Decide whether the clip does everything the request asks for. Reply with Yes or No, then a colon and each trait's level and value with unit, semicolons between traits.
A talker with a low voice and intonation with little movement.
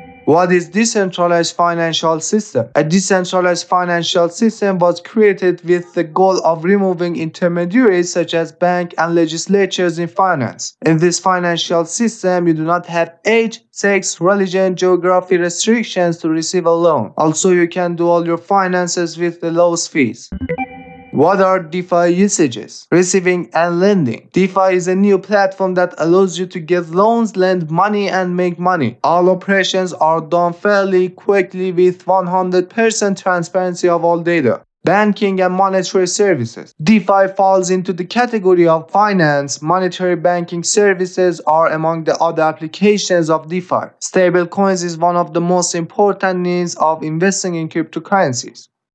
No: medium, 180 Hz; narrow, 2.1 semitones